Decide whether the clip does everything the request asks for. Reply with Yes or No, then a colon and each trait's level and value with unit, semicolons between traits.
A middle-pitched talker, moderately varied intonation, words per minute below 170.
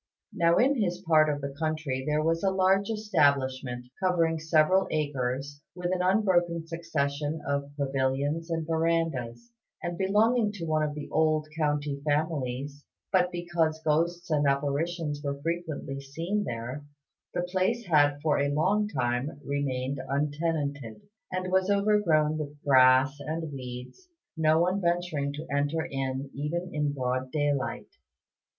Yes: medium, 155 Hz; average, 3.5 semitones; average, 140 wpm